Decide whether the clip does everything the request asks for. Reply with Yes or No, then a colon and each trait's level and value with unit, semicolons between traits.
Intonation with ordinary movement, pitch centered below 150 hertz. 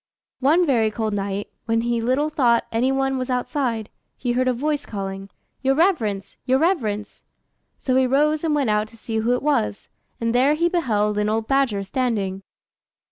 No: average, 4.2 semitones; high, 245 Hz